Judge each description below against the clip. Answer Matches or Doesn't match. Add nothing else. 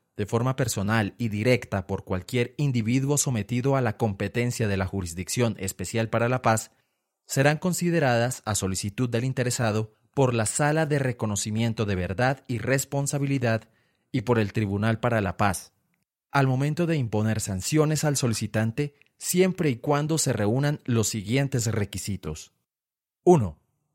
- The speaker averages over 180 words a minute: Doesn't match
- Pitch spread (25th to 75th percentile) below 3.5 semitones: Doesn't match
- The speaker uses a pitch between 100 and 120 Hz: Matches